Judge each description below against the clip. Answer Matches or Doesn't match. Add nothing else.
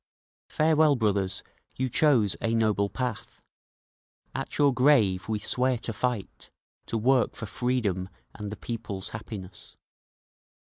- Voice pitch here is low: Matches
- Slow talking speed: Matches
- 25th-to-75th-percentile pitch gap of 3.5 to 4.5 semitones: Matches